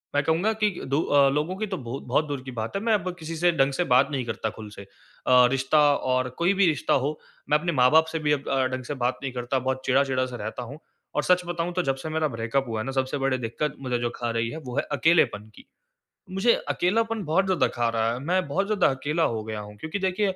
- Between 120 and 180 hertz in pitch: Yes, medium, 140 Hz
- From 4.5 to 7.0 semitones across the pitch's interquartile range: Yes, average, 5.2 semitones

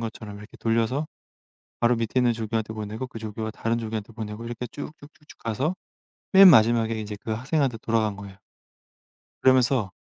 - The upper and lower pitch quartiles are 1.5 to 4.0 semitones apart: Yes, narrow, 2.6 semitones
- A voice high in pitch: No, low, 115 Hz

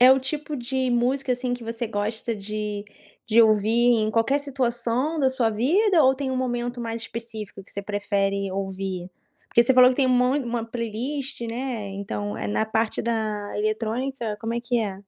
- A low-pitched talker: No, high, 235 Hz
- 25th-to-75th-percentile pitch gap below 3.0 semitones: No, average, 3.3 semitones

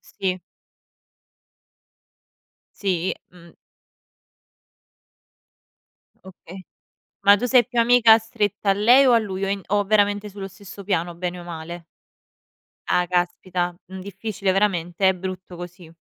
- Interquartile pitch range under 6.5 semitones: Yes, narrow, 2.5 semitones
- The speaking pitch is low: No, high, 190 Hz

